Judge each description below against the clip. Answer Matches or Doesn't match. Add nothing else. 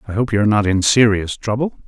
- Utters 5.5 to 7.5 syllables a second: Matches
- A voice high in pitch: Doesn't match